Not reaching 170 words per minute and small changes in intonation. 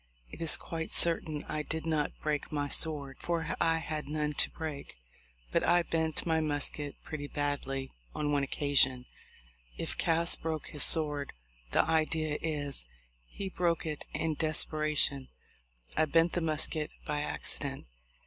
Yes: average, 150 wpm; narrow, 1.9 semitones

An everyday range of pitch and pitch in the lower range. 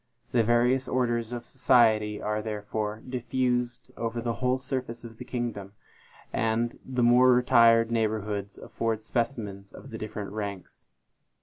No: narrow, 2.3 semitones; low, 115 Hz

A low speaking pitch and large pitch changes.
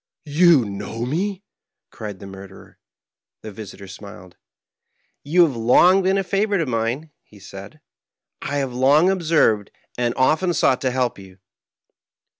Yes: low, 130 Hz; wide, 7.8 semitones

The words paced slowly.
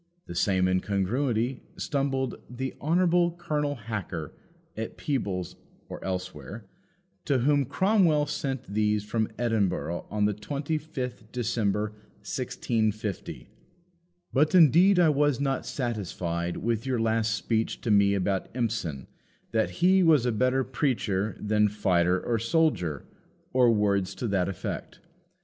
Yes: slow, 125 wpm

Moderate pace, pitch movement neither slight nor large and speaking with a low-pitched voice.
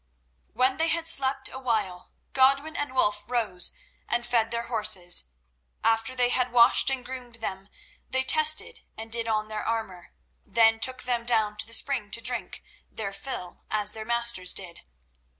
No: average, 165 wpm; average, 3.3 semitones; high, 235 Hz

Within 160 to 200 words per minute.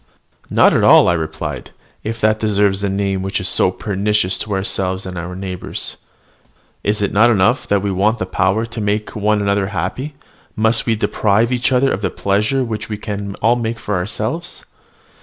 Yes: average, 190 wpm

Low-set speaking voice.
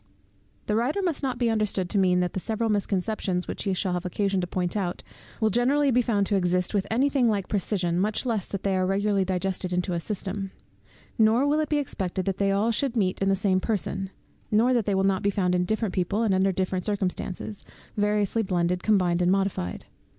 No: high, 195 Hz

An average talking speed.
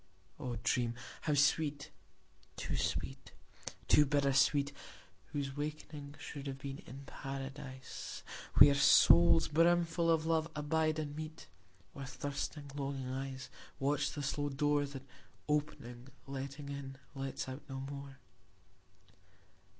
No: slow, 120 wpm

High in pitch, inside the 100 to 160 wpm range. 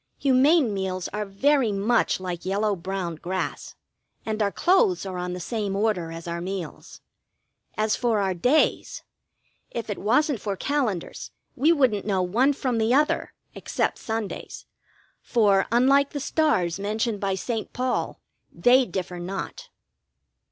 Yes: high, 210 Hz; average, 145 wpm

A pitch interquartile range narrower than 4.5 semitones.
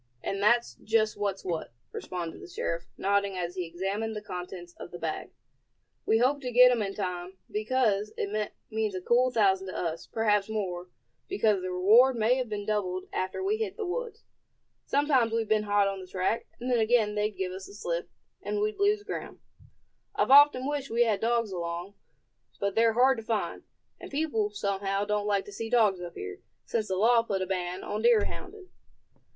Yes: average, 3.9 semitones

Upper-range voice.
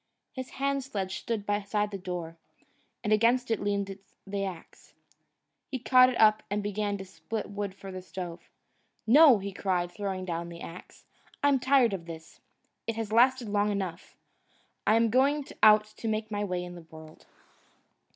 Yes: high, 205 Hz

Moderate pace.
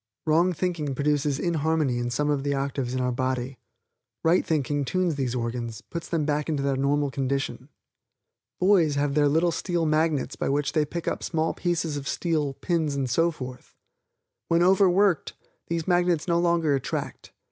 Yes: average, 170 wpm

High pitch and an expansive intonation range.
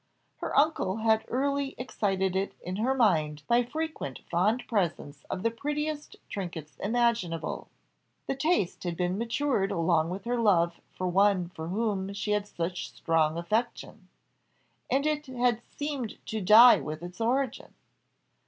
Yes: high, 205 Hz; wide, 5.8 semitones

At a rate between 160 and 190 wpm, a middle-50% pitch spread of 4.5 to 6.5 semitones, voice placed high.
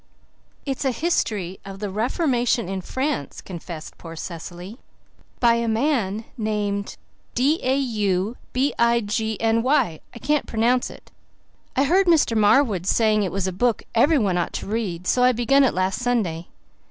Yes: average, 165 wpm; average, 4.9 semitones; high, 225 Hz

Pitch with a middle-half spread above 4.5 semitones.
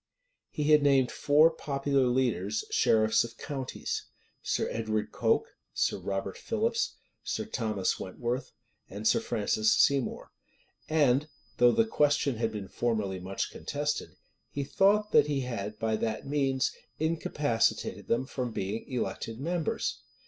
Yes: average, 5.0 semitones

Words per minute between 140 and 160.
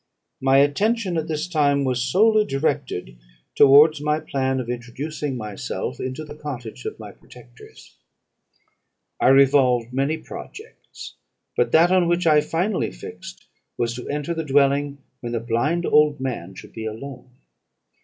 Yes: average, 145 wpm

